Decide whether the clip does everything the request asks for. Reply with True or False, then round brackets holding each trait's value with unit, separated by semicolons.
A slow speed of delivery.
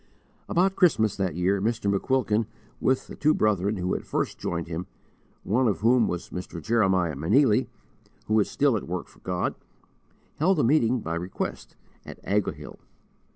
False (160 wpm)